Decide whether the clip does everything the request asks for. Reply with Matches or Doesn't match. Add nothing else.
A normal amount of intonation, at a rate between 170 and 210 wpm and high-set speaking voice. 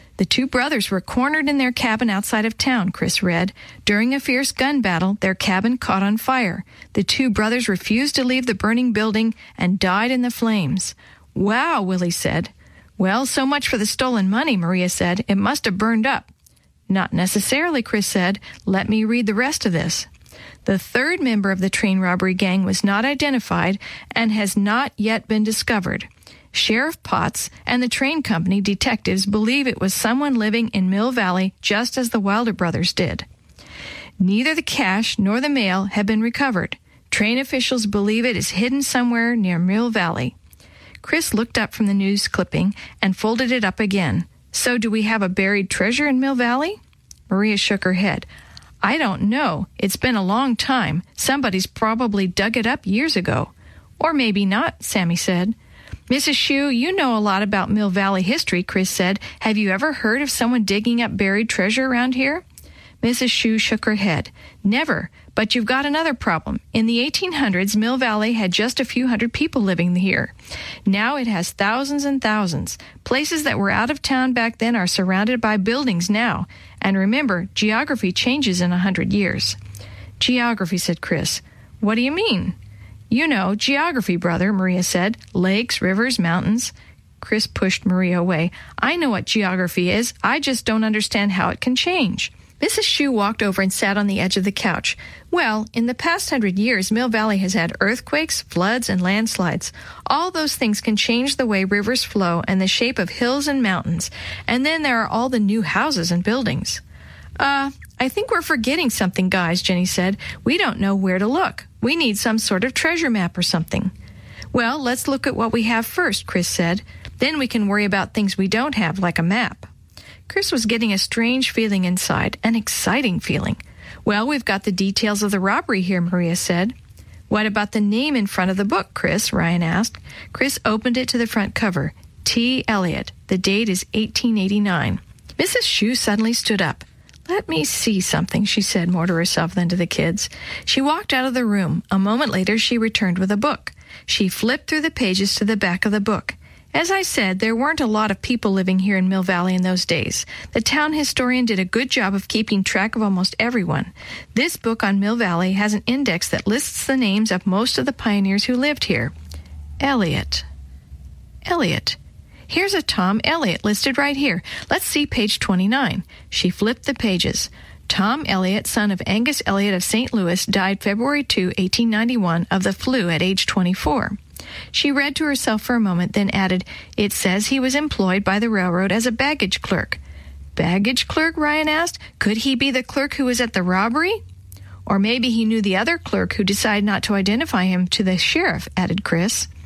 Matches